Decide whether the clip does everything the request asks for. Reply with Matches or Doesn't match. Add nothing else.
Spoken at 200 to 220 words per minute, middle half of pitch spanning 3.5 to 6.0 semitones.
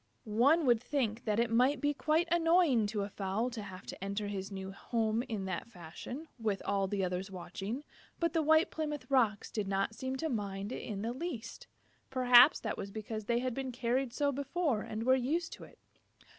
Matches